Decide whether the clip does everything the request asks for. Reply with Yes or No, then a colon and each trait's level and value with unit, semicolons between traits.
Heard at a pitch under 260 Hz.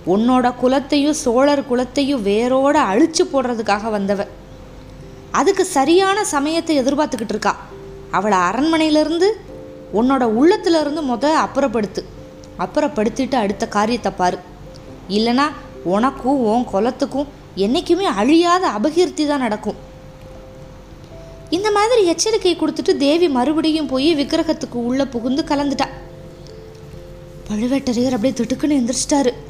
No: very high, 275 Hz